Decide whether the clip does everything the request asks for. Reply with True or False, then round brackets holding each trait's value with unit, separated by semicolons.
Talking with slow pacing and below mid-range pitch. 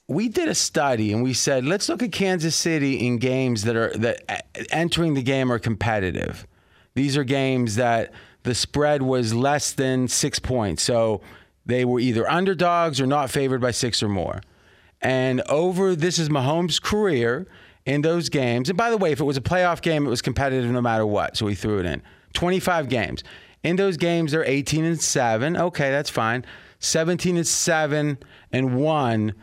False (190 wpm; 130 Hz)